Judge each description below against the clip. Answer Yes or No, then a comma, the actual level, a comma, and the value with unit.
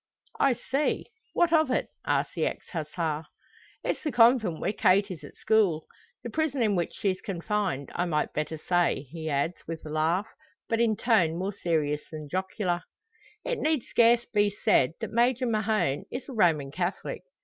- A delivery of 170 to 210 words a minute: Yes, average, 175 wpm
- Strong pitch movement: Yes, wide, 6.2 semitones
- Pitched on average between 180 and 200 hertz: Yes, high, 190 Hz